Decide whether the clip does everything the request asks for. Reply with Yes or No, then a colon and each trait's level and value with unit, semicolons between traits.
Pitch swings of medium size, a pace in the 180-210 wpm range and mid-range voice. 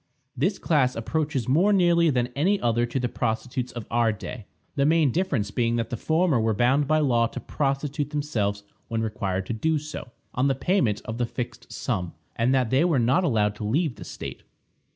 No: average, 4.8 semitones; average, 200 wpm; low, 125 Hz